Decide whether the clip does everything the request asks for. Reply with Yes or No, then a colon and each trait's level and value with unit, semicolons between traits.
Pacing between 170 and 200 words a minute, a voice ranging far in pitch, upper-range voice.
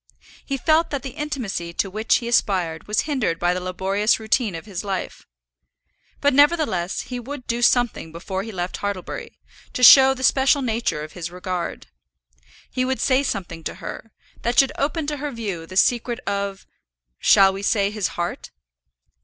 Yes: average, 175 wpm; wide, 6.1 semitones; high, 215 Hz